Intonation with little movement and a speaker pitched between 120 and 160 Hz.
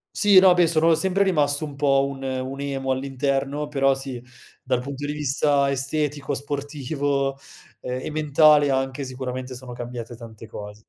Yes: narrow, 2.1 semitones; medium, 140 Hz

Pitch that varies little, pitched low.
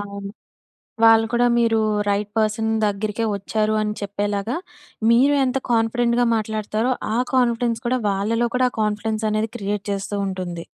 No: narrow, 2.3 semitones; high, 215 Hz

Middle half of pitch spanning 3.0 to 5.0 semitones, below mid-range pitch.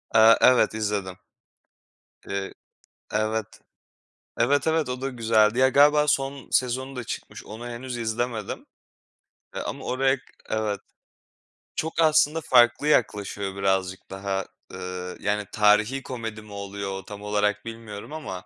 Yes: average, 4.2 semitones; low, 110 Hz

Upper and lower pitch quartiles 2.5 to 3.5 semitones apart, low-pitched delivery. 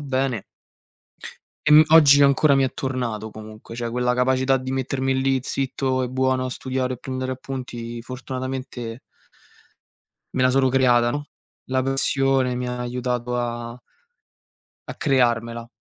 No: narrow, 1.5 semitones; low, 130 Hz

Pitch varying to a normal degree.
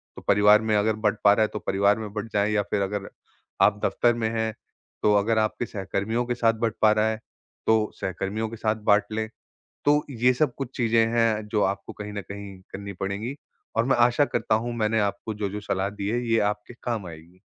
No: narrow, 1.9 semitones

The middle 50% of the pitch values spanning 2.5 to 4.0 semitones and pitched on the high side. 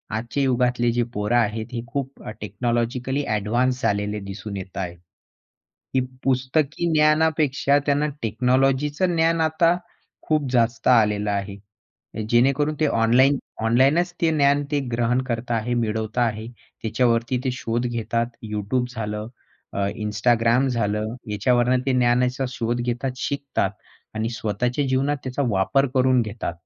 No: average, 3.5 semitones; low, 120 Hz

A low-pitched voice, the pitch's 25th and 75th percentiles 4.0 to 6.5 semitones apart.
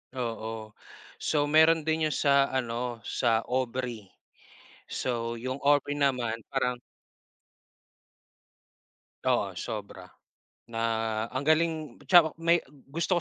Yes: low, 130 Hz; average, 4.9 semitones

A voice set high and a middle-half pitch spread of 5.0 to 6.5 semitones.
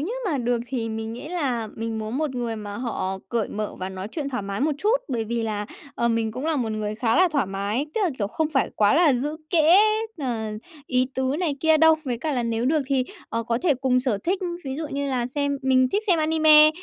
Yes: very high, 255 Hz; average, 5.3 semitones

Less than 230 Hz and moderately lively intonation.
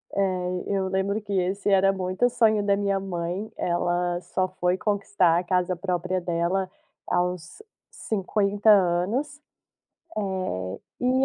No: high, 190 Hz; narrow, 2.1 semitones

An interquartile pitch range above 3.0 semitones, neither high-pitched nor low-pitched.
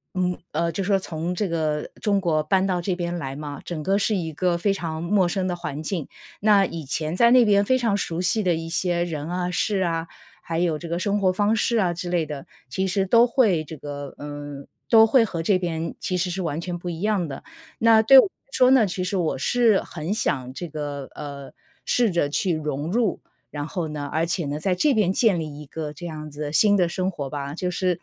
Yes: average, 4.1 semitones; medium, 175 Hz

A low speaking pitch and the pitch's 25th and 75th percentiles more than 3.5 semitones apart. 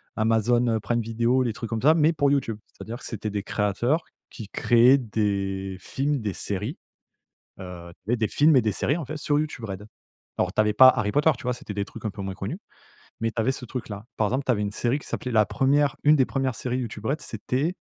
Yes: low, 115 Hz; average, 4.2 semitones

